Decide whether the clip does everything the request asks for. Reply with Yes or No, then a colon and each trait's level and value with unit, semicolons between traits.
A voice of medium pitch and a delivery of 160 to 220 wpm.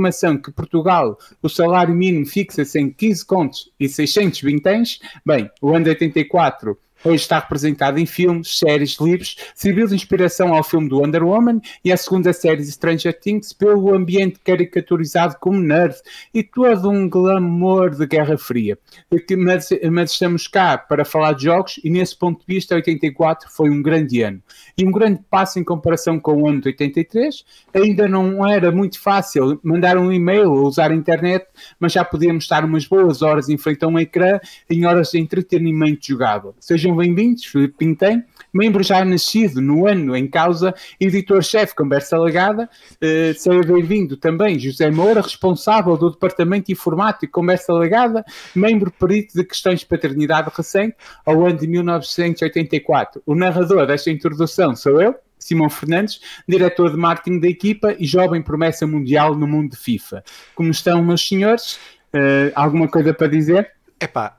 Yes: medium, 175 Hz; average, 165 wpm